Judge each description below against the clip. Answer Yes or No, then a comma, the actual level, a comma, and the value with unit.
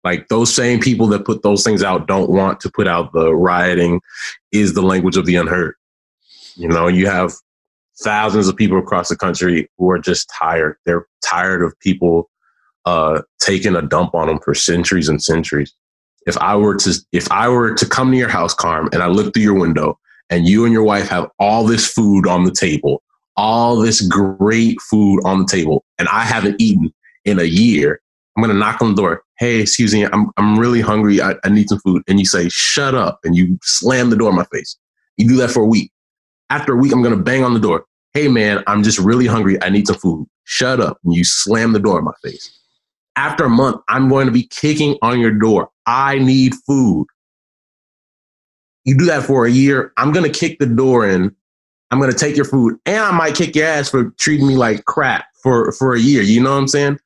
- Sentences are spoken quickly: Yes, fast, 225 wpm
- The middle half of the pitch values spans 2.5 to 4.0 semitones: No, average, 5.0 semitones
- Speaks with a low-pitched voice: Yes, low, 105 Hz